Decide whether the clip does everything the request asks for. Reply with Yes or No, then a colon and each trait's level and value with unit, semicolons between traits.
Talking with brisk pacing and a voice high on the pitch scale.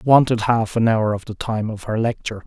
No: fast, 270 wpm; low, 110 Hz